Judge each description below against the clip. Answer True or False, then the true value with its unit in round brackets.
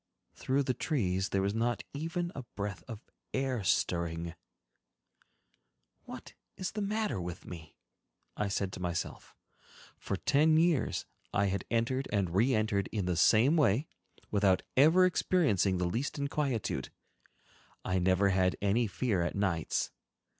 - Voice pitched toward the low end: True (105 Hz)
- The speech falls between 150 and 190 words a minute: False (140 wpm)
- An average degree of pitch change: False (6.8 semitones)